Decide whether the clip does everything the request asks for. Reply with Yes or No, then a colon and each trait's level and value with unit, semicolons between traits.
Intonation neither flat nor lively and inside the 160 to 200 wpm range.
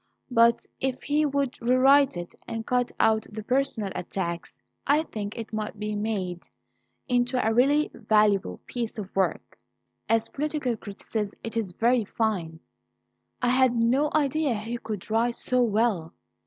No: average, 3.3 semitones; average, 150 wpm